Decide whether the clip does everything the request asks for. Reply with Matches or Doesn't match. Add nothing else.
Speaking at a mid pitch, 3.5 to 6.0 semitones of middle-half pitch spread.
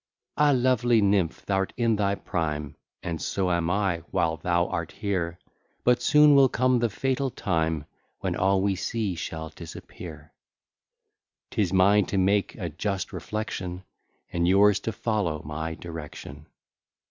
Doesn't match